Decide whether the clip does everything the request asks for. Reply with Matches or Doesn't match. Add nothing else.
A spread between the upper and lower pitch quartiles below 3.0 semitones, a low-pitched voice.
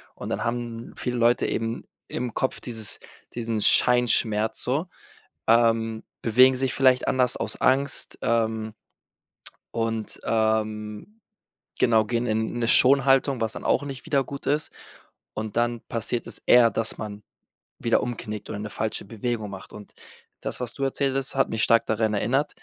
Matches